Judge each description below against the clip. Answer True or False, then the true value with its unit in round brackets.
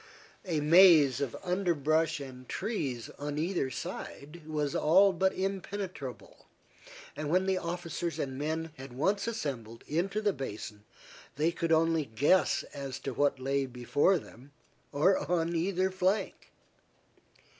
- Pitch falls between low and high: True (160 Hz)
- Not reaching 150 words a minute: True (135 wpm)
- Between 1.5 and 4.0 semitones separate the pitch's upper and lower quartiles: False (5.0 semitones)